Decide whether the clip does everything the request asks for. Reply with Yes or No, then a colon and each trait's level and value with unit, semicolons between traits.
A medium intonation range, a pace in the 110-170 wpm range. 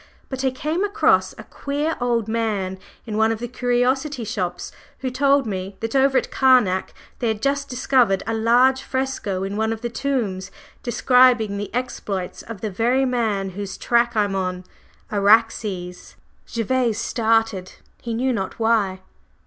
Yes: average, 4.2 semitones; average, 160 wpm